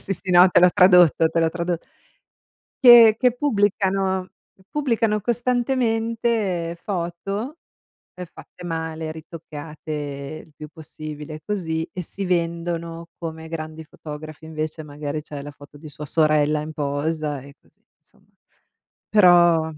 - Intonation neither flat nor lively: Yes, average, 3.7 semitones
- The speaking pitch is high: No, medium, 165 Hz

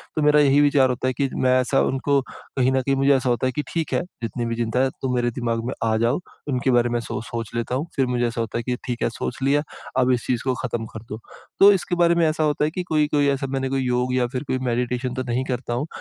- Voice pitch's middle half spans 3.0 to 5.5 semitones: No, narrow, 2.4 semitones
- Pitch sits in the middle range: No, low, 130 Hz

